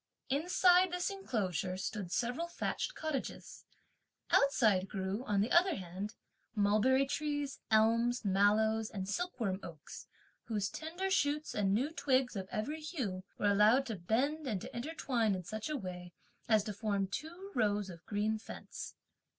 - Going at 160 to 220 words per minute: No, average, 150 wpm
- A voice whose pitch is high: Yes, high, 220 Hz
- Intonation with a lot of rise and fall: Yes, wide, 6.5 semitones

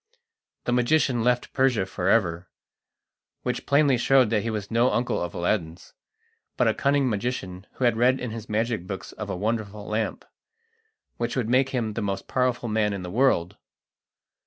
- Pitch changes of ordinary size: Yes, average, 3.8 semitones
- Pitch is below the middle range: Yes, low, 115 Hz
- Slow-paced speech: No, average, 175 wpm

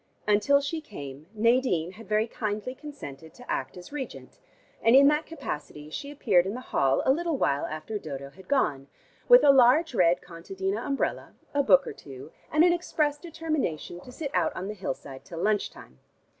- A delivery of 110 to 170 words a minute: No, average, 185 wpm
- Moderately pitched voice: No, high, 215 Hz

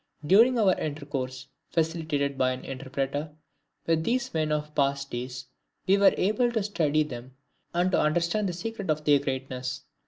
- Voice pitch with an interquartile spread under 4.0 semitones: No, average, 5.0 semitones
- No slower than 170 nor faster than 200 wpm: No, average, 160 wpm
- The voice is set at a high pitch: No, medium, 150 Hz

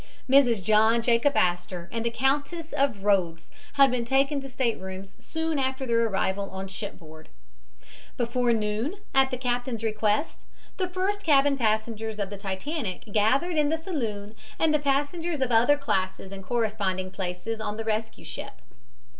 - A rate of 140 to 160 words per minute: Yes, average, 155 wpm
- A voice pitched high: Yes, high, 230 Hz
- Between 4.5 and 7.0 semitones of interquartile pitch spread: Yes, average, 5.3 semitones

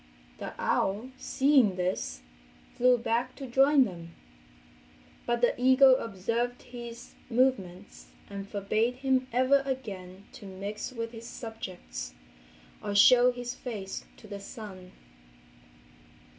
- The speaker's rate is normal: No, slow, 115 wpm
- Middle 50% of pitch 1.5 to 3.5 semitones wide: No, average, 4.2 semitones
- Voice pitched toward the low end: No, high, 230 Hz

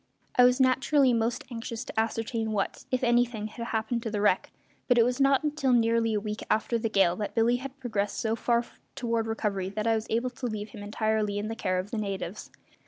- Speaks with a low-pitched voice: No, high, 225 Hz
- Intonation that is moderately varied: No, narrow, 2.3 semitones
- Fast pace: Yes, fast, 225 wpm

